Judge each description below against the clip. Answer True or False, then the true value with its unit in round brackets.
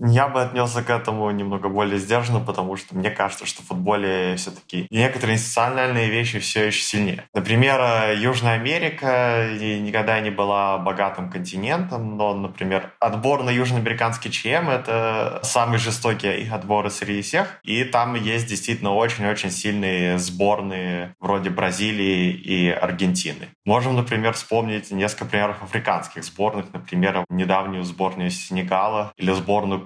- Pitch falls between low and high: False (105 Hz)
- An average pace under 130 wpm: False (135 wpm)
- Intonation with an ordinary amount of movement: True (3.2 semitones)